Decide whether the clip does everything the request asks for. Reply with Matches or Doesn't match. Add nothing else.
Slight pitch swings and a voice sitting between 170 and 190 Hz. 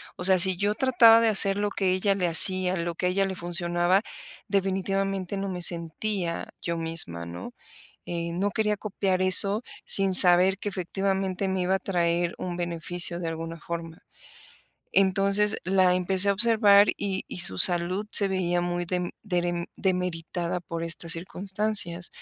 Matches